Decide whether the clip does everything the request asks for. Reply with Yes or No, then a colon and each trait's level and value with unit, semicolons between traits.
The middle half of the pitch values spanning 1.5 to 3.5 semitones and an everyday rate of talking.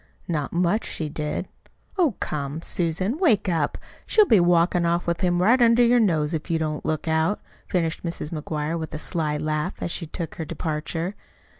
Yes: average, 3.1 semitones; average, 185 wpm